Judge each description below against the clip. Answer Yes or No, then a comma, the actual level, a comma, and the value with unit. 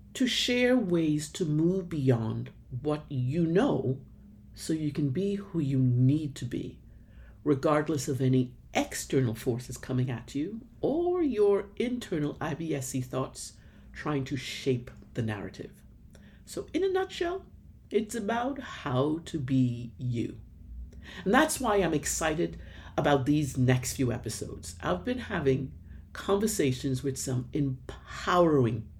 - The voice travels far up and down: Yes, wide, 5.8 semitones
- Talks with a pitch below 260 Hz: Yes, medium, 140 Hz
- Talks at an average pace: No, slow, 130 wpm